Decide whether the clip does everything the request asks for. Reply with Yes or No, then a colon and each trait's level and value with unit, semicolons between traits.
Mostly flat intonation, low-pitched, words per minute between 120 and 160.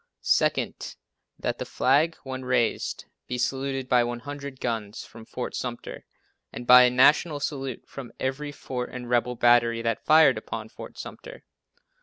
Yes: narrow, 2.3 semitones; low, 125 Hz; average, 150 wpm